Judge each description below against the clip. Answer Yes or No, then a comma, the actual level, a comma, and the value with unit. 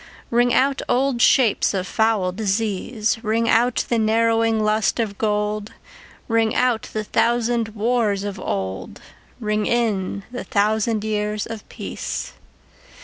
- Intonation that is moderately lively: No, narrow, 1.9 semitones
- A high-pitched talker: Yes, high, 220 Hz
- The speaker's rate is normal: No, slow, 130 wpm